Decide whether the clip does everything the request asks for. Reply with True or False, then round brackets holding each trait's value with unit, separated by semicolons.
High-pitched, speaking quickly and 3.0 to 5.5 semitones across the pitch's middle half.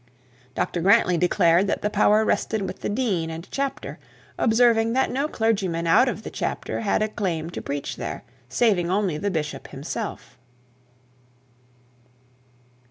False (200 Hz; 145 wpm; 5.0 semitones)